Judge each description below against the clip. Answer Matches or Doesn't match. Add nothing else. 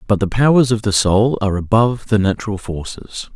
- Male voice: Matches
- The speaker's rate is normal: Matches